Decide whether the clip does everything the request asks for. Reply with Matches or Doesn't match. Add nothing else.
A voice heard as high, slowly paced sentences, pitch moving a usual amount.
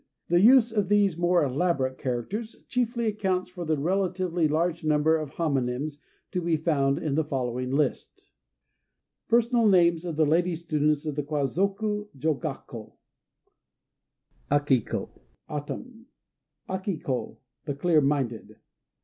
Doesn't match